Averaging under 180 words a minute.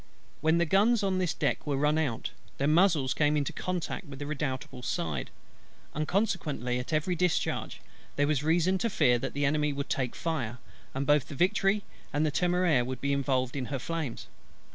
No: average, 185 wpm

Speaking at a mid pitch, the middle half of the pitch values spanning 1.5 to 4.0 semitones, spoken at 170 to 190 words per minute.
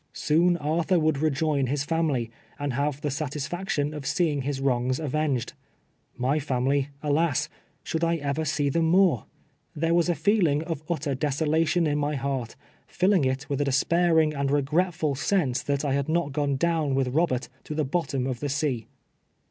Yes: medium, 150 Hz; average, 3.0 semitones; average, 180 wpm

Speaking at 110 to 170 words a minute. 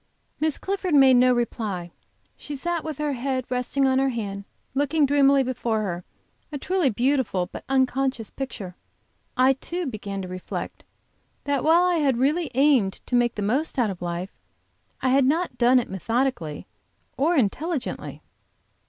Yes: average, 160 wpm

